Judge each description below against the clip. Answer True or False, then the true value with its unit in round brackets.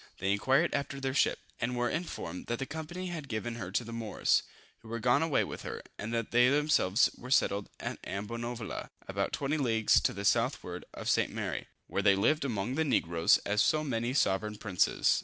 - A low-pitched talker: True (120 Hz)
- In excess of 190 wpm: True (200 wpm)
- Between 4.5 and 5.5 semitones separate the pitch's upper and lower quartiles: True (4.9 semitones)